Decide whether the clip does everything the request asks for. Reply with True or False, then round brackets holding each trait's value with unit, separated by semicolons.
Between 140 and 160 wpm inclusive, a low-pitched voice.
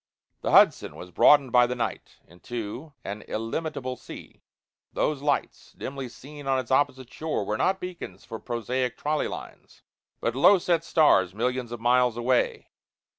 True (155 wpm; 125 Hz)